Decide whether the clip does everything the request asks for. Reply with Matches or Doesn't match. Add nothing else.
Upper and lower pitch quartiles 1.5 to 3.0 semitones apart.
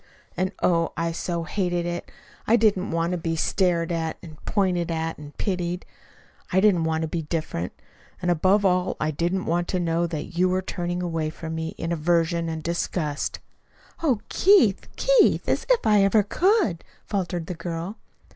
Matches